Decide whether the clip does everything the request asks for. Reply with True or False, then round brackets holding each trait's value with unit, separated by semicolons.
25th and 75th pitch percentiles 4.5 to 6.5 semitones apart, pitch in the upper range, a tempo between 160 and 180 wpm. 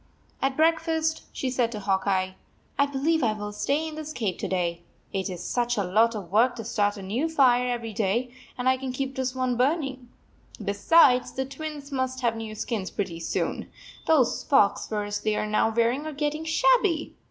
False (5.1 semitones; 250 Hz; 200 wpm)